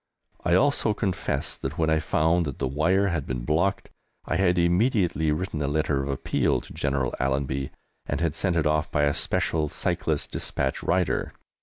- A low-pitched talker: Yes, very low, 80 Hz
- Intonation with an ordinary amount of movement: Yes, average, 4.1 semitones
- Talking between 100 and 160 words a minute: No, average, 180 wpm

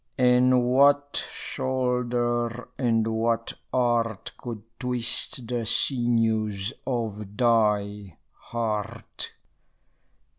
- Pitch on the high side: No, low, 120 Hz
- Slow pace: Yes, slow, 75 wpm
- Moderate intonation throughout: No, narrow, 2.0 semitones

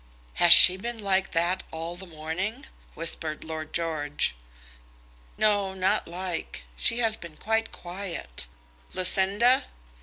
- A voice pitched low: No, medium, 180 Hz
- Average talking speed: No, slow, 120 wpm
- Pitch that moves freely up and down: No, average, 3.7 semitones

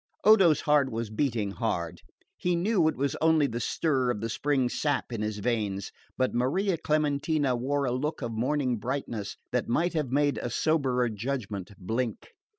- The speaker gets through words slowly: No, average, 170 wpm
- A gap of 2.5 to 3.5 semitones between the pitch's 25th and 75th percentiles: No, average, 4.6 semitones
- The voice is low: Yes, low, 130 Hz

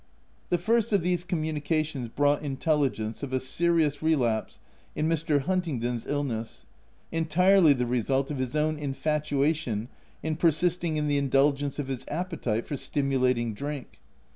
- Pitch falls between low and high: Yes, medium, 145 Hz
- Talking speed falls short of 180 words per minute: Yes, average, 140 wpm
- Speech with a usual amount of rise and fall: Yes, average, 3.4 semitones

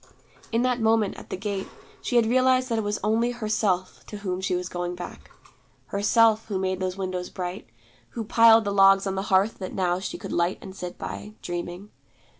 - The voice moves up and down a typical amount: Yes, average, 3.2 semitones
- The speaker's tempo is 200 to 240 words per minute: Yes, fast, 205 wpm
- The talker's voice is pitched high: Yes, high, 200 Hz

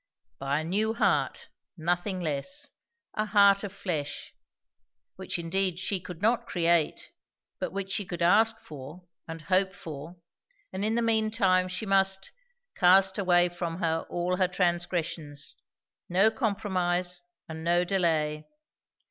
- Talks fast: No, average, 140 wpm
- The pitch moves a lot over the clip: No, average, 2.9 semitones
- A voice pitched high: No, medium, 180 Hz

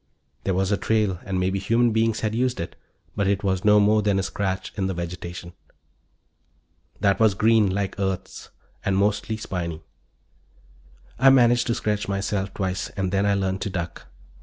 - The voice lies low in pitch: Yes, low, 100 Hz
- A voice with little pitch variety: Yes, narrow, 2.1 semitones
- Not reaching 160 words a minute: No, average, 175 wpm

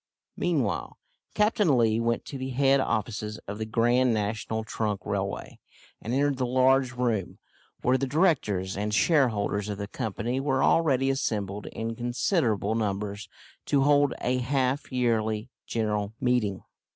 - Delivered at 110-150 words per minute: Yes, average, 140 wpm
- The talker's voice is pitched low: Yes, low, 120 Hz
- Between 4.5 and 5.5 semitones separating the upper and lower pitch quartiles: No, average, 4.0 semitones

